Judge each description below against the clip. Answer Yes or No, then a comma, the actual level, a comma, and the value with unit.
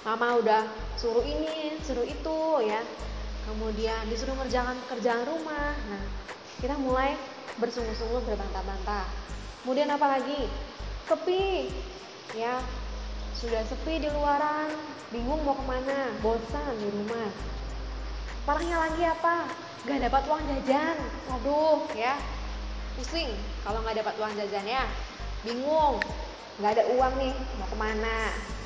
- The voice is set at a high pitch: Yes, very high, 255 Hz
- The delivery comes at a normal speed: Yes, average, 115 wpm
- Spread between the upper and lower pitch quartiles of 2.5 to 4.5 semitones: No, average, 5.0 semitones